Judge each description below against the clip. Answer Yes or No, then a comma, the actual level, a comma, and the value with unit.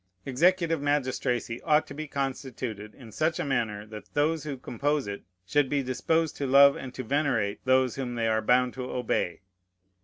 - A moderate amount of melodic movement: Yes, average, 3.3 semitones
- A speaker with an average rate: Yes, average, 180 wpm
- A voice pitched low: Yes, low, 130 Hz